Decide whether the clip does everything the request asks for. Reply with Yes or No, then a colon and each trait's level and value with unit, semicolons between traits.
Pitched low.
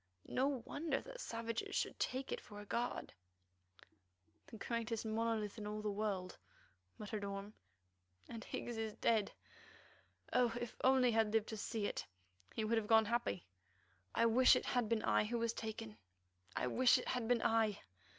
No: high, 225 Hz